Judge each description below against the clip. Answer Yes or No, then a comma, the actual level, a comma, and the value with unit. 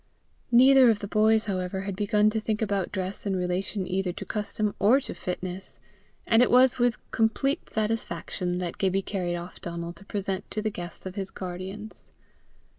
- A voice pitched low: No, high, 200 Hz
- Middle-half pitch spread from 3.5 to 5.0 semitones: No, average, 3.0 semitones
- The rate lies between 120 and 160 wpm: No, average, 180 wpm